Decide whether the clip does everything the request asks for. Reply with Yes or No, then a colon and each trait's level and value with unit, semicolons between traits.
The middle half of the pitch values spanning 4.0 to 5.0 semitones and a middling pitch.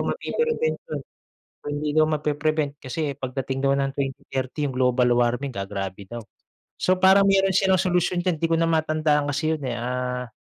Yes: average, 4.5 semitones; medium, 145 Hz